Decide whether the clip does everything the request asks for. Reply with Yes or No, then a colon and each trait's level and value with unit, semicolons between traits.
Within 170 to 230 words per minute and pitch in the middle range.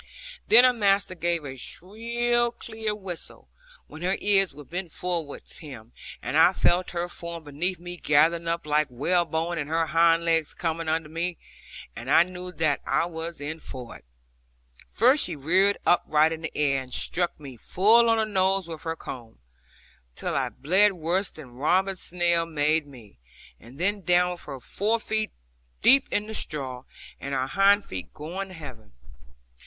Yes: average, 175 wpm; medium, 170 Hz